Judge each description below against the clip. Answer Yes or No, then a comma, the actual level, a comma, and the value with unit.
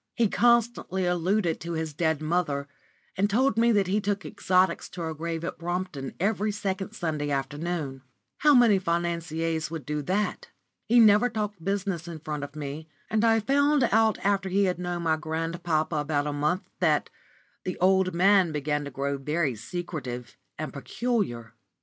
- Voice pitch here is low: No, medium, 175 Hz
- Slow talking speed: No, average, 165 wpm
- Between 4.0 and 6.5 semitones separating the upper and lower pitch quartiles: Yes, average, 4.7 semitones